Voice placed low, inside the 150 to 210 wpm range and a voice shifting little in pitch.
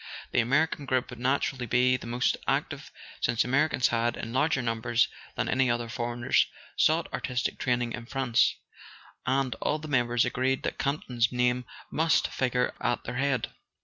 Yes: low, 125 Hz; average, 165 wpm; narrow, 2.0 semitones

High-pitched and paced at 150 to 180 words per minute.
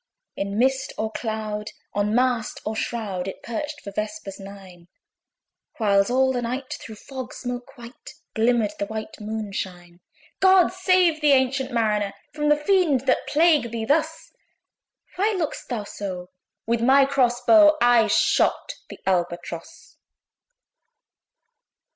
No: high, 235 Hz; slow, 135 wpm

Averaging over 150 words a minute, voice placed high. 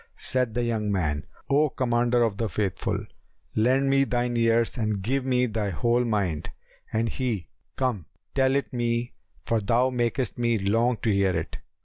No: average, 165 wpm; low, 115 Hz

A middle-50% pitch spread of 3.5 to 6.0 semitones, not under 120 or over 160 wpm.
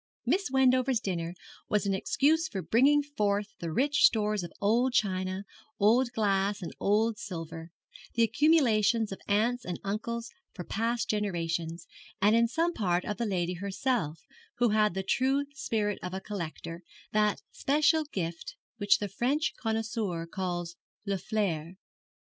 Yes: average, 4.5 semitones; average, 150 wpm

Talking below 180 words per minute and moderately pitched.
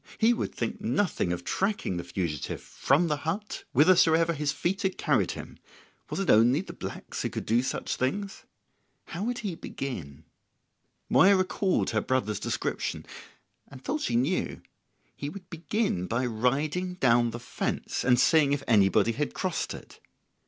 Yes: average, 160 wpm; medium, 150 Hz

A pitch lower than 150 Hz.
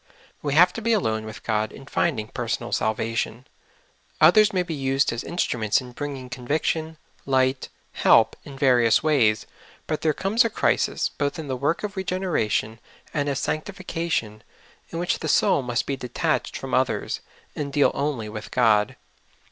Yes: medium, 140 Hz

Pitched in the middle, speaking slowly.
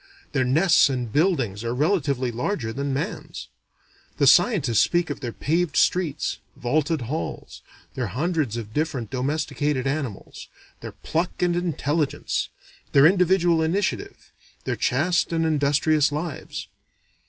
Yes: medium, 150 Hz; slow, 125 wpm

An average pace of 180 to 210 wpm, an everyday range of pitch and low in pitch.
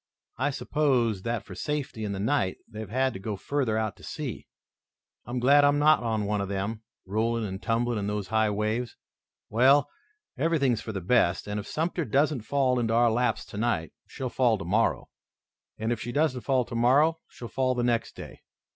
Yes: average, 190 wpm; average, 3.8 semitones; low, 115 Hz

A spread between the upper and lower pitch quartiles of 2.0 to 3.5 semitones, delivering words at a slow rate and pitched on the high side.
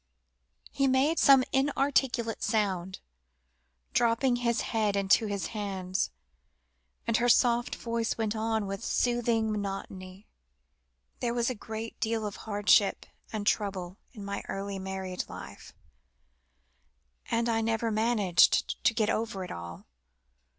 Yes: average, 3.0 semitones; slow, 125 wpm; high, 220 Hz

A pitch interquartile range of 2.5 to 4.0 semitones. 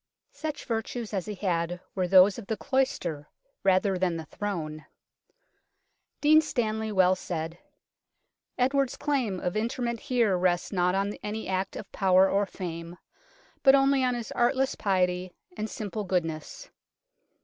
No: average, 4.9 semitones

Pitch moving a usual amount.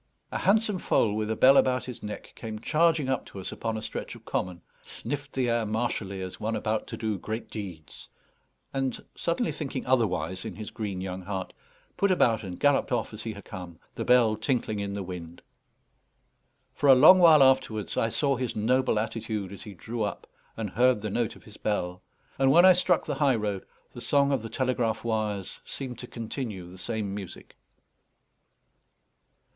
Yes: average, 4.3 semitones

